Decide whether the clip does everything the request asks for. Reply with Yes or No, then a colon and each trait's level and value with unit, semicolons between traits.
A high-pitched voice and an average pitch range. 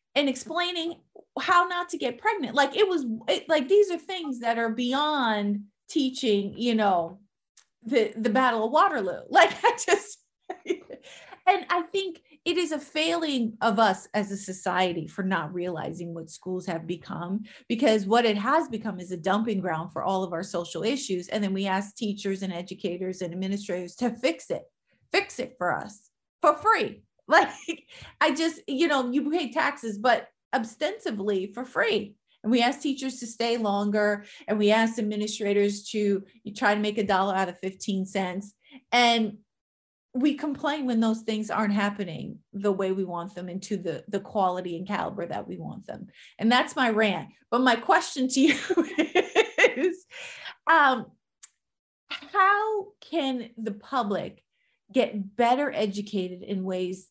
No: high, 225 Hz; wide, 7.2 semitones